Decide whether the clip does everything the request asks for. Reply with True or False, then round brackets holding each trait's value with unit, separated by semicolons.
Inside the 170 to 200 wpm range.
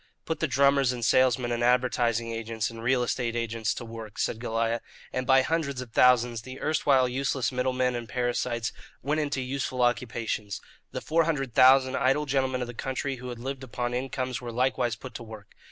True (190 wpm)